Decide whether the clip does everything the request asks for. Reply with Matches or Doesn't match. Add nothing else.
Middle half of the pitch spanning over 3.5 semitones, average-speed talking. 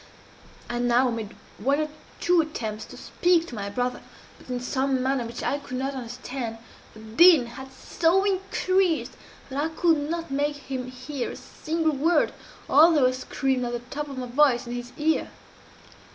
Matches